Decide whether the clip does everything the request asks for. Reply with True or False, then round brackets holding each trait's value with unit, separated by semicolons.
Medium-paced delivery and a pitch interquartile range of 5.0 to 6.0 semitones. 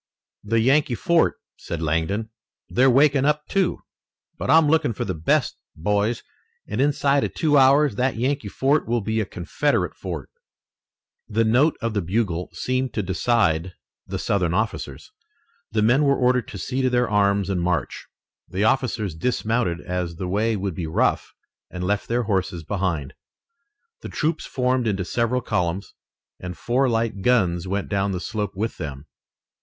True (165 wpm; 5.4 semitones)